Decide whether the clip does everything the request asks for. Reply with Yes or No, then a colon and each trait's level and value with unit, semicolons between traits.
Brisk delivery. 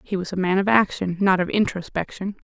Yes: fast, 220 wpm